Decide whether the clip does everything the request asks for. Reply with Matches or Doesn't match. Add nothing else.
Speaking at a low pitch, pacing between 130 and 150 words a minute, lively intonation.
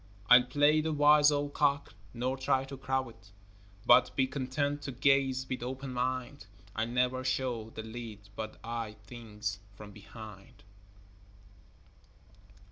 Doesn't match